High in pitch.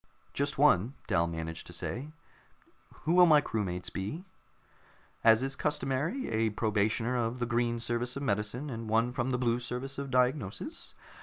No: low, 120 Hz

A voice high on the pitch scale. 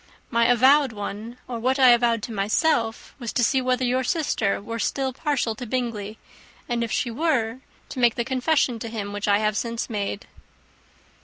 Yes: high, 235 Hz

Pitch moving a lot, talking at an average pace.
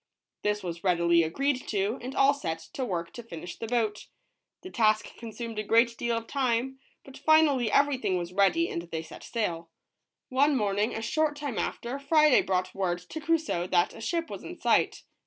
Yes: wide, 6.8 semitones; average, 190 wpm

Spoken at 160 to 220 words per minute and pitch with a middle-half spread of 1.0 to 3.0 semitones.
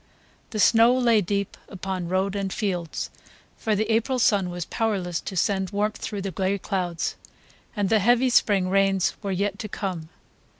Yes: average, 170 wpm; narrow, 2.5 semitones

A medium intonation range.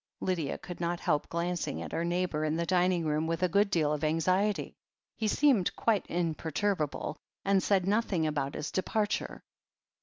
Yes: average, 3.5 semitones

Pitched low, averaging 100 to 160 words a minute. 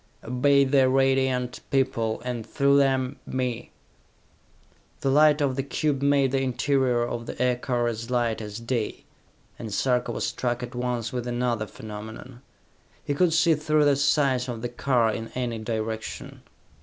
Yes: low, 125 Hz; average, 155 wpm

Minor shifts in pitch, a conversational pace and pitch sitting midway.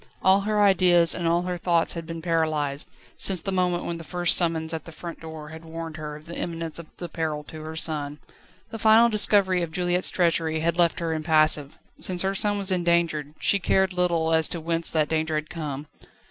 No: narrow, 2.1 semitones; fast, 215 wpm; medium, 165 Hz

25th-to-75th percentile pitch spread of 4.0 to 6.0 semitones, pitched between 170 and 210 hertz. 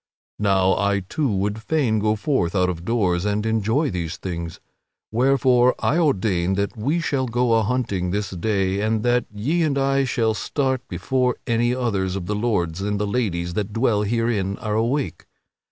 No: average, 4.3 semitones; low, 110 Hz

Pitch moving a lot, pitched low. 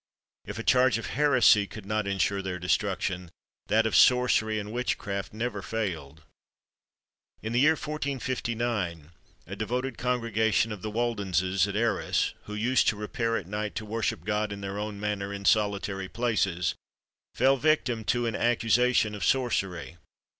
No: average, 3.3 semitones; low, 110 Hz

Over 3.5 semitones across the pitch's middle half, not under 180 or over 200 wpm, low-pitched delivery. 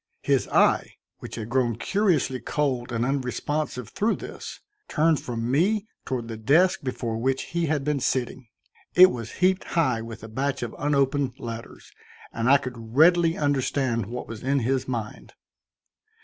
No: average, 4.1 semitones; average, 160 wpm; low, 130 Hz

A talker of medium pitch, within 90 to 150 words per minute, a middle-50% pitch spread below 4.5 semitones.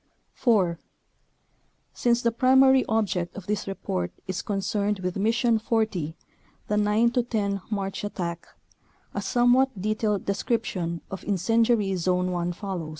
No: high, 205 Hz; slow, 135 wpm; average, 3.9 semitones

